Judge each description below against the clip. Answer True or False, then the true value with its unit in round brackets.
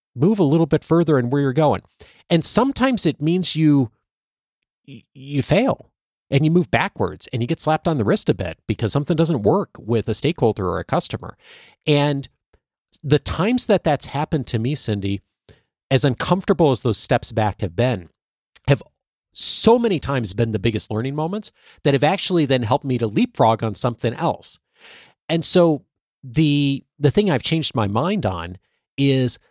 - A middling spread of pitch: False (5.9 semitones)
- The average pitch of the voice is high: False (140 Hz)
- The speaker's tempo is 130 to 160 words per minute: False (175 wpm)